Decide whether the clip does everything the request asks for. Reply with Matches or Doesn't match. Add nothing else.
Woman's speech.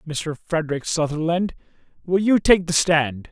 Doesn't match